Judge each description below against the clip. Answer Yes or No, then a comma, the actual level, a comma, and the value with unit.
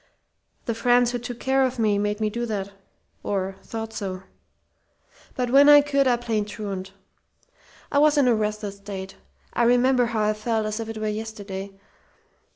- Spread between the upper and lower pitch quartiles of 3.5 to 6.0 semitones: No, average, 3.0 semitones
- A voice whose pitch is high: Yes, high, 220 Hz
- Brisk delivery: No, average, 175 wpm